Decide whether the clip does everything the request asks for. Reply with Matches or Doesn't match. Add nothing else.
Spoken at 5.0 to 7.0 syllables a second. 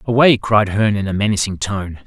Matches